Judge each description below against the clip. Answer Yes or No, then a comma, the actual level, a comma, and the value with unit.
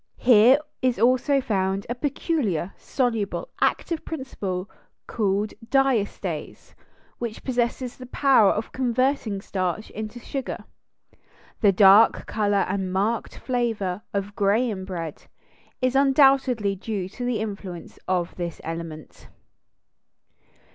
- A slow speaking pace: Yes, slow, 110 wpm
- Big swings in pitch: No, average, 4.7 semitones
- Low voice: No, high, 215 Hz